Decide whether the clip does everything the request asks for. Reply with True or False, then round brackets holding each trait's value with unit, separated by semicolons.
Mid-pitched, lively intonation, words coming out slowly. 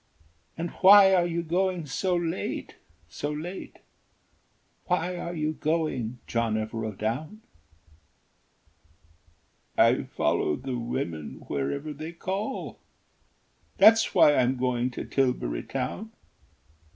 True (150 Hz; 6.5 semitones; 105 wpm)